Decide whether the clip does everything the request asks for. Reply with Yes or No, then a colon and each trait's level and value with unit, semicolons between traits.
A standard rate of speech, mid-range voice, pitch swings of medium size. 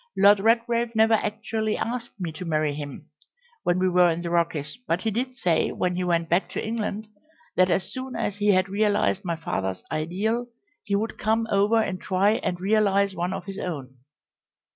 No: average, 190 wpm; high, 195 Hz; average, 4.0 semitones